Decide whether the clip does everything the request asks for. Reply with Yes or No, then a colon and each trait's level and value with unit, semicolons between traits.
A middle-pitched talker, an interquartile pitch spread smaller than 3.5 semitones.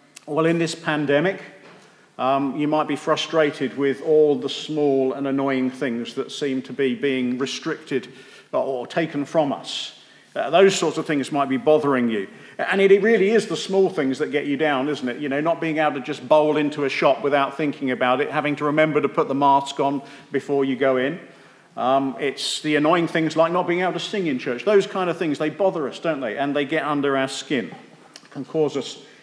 Yes: medium, 145 Hz; narrow, 2.5 semitones